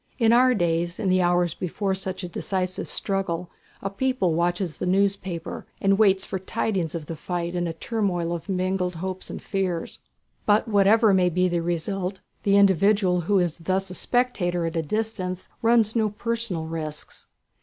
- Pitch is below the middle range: No, medium, 185 Hz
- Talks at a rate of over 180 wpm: No, average, 175 wpm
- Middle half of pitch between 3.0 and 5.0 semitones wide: No, narrow, 2.5 semitones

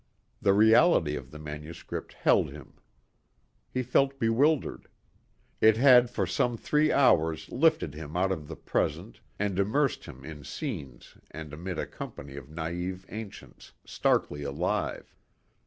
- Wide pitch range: Yes, wide, 8.1 semitones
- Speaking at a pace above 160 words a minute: No, average, 140 wpm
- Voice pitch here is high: No, very low, 95 Hz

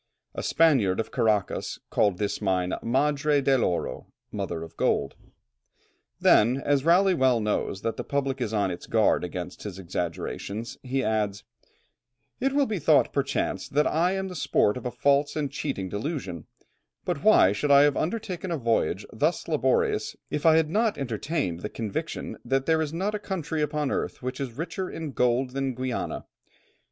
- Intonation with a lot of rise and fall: Yes, wide, 6.4 semitones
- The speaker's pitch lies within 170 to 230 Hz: No, low, 135 Hz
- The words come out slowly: No, average, 175 wpm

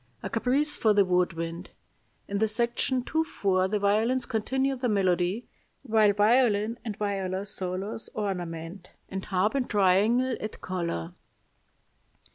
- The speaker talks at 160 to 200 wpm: No, slow, 135 wpm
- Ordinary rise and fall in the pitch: Yes, average, 3.9 semitones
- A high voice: Yes, high, 205 Hz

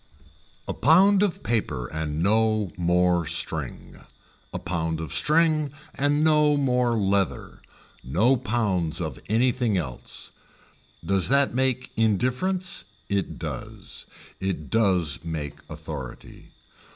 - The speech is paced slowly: Yes, slow, 110 wpm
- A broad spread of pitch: Yes, wide, 7.7 semitones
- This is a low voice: Yes, low, 110 Hz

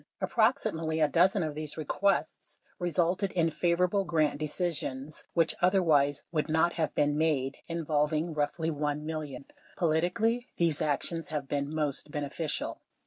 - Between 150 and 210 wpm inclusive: No, slow, 135 wpm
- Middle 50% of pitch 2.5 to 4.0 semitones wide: Yes, average, 2.8 semitones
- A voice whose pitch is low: No, medium, 160 Hz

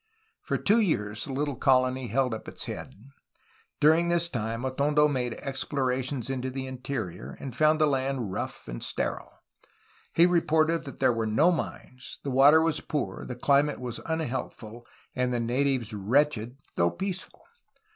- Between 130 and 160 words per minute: Yes, average, 155 wpm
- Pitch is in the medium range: No, low, 130 Hz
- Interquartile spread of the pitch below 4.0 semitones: Yes, average, 3.6 semitones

